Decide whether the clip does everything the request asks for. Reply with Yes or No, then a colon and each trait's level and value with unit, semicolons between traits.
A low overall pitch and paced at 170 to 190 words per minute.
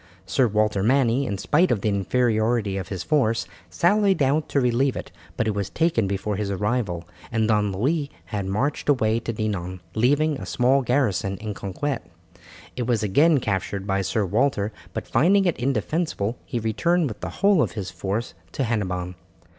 Yes: low, 115 Hz; average, 180 wpm